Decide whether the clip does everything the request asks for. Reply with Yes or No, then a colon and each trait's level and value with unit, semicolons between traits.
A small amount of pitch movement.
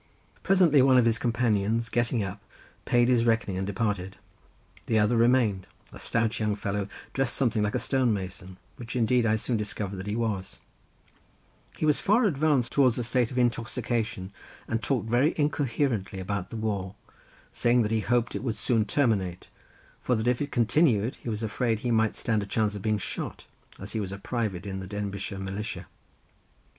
No: average, 3.2 semitones